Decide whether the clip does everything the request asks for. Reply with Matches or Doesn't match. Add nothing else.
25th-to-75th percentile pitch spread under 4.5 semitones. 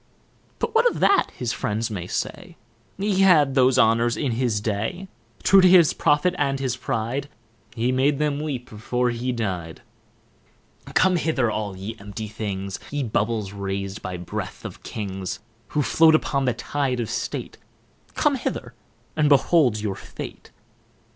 Doesn't match